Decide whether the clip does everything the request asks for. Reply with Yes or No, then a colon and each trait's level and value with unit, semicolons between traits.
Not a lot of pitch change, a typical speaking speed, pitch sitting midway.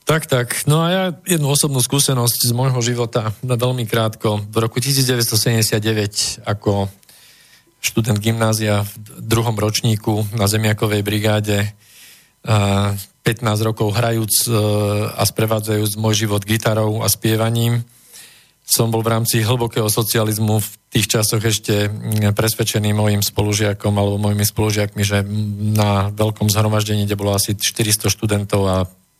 No: narrow, 1.8 semitones; average, 125 wpm; low, 110 Hz